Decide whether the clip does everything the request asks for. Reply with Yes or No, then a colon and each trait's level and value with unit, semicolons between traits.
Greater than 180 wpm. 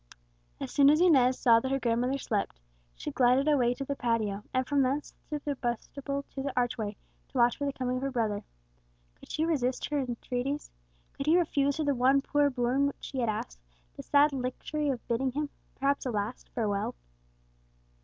Yes: average, 195 wpm